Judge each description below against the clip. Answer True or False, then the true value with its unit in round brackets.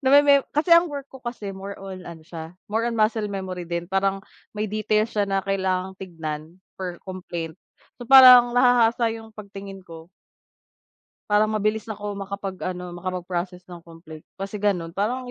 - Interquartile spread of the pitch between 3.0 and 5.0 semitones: True (3.7 semitones)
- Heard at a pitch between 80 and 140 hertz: False (195 Hz)